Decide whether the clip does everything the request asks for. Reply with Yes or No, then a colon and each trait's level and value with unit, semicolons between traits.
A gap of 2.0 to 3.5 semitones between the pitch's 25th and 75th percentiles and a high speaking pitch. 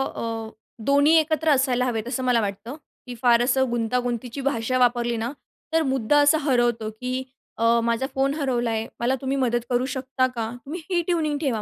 Yes: average, 2.8 semitones; very high, 250 Hz